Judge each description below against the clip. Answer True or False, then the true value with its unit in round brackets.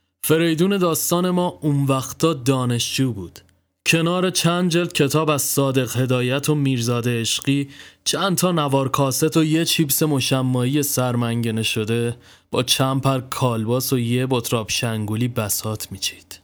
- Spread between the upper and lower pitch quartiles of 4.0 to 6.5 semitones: True (4.7 semitones)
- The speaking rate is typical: True (135 wpm)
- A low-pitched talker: True (130 Hz)